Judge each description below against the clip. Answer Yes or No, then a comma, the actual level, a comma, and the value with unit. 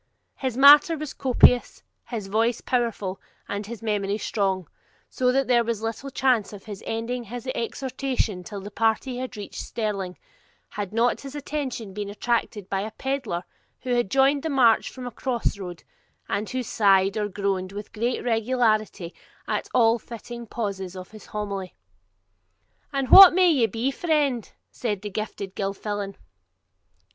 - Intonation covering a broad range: No, average, 3.9 semitones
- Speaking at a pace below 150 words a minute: No, average, 155 wpm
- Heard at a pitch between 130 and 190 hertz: No, high, 225 Hz